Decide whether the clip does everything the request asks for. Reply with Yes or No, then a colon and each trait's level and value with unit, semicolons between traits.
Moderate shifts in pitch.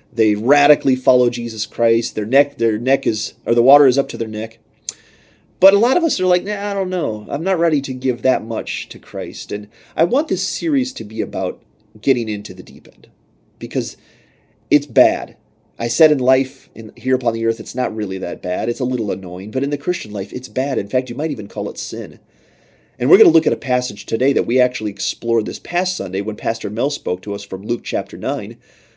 Yes: average, 4.5 semitones